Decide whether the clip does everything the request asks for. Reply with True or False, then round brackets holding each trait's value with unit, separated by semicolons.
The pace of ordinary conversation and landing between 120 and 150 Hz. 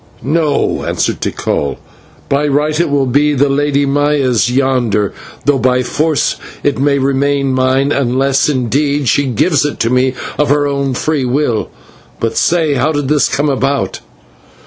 True (155 wpm; 140 Hz)